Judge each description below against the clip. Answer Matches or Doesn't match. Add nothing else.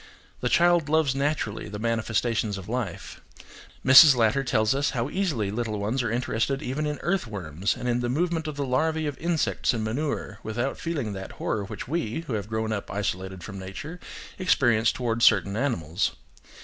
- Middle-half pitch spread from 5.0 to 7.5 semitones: Matches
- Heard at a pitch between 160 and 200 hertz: Doesn't match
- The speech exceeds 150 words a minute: Matches